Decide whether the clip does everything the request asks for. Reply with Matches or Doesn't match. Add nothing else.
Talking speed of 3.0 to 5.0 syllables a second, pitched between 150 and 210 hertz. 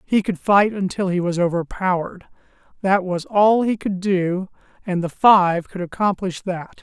Matches